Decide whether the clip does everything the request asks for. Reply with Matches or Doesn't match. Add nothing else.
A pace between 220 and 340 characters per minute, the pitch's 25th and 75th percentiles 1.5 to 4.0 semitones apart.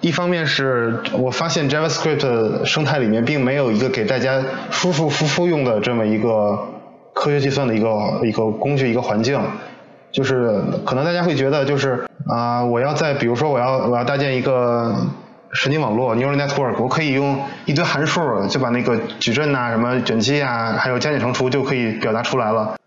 Doesn't match